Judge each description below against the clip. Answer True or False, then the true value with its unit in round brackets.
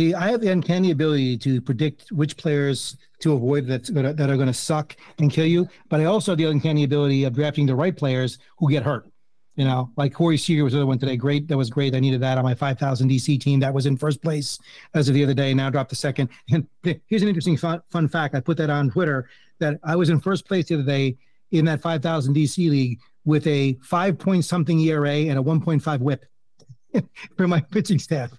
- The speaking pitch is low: False (145 Hz)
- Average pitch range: True (3.2 semitones)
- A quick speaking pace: True (240 wpm)